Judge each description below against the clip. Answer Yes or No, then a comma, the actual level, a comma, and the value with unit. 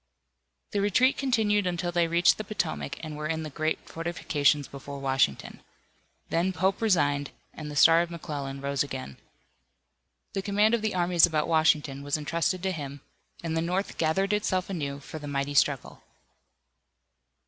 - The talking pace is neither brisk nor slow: Yes, average, 160 wpm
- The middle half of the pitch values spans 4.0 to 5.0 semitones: Yes, average, 4.5 semitones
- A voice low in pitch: No, medium, 165 Hz